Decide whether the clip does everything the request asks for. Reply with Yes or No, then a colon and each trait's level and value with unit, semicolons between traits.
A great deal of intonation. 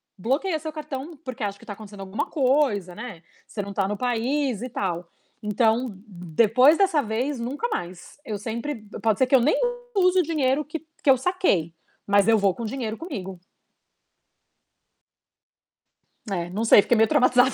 Yes: wide, 5.7 semitones